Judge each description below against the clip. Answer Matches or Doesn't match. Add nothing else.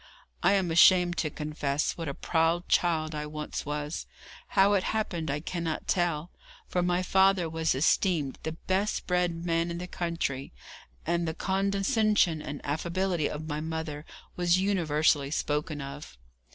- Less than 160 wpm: Matches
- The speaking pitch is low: Doesn't match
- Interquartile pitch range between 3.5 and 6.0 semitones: Doesn't match